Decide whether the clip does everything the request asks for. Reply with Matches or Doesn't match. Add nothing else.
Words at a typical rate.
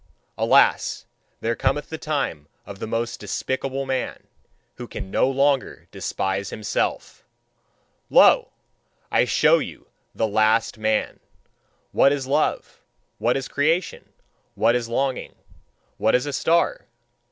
Doesn't match